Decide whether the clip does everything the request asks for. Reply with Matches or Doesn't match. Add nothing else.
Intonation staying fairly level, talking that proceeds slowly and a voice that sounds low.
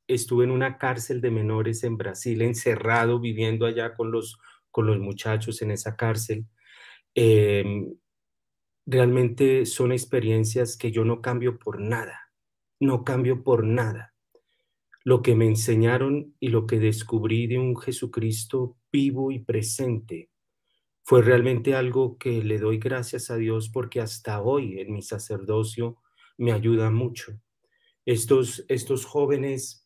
Doesn't match